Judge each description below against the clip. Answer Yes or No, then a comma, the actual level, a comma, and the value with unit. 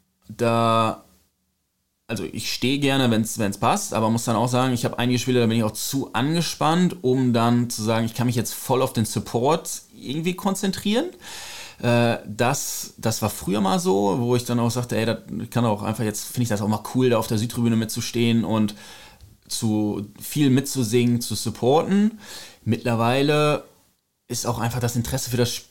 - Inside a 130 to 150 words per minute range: No, average, 185 wpm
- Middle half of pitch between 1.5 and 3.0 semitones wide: Yes, narrow, 2.4 semitones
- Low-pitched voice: Yes, low, 120 Hz